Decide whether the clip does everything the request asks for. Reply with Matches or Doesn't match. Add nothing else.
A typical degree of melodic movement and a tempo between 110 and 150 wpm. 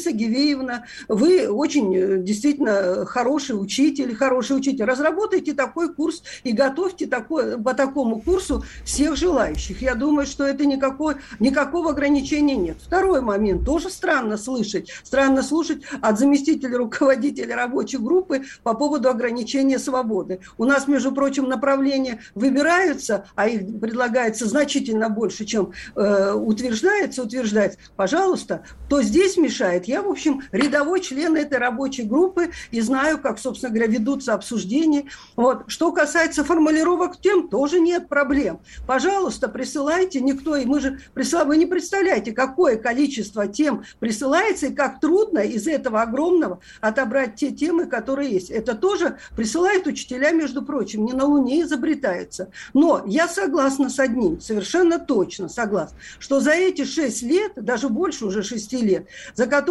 Matches